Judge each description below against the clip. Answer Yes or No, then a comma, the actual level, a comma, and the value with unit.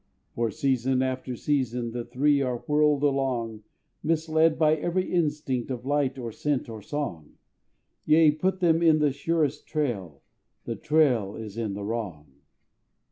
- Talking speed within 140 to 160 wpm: Yes, average, 145 wpm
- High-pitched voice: No, low, 135 Hz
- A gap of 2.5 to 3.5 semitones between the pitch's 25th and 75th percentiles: No, average, 4.6 semitones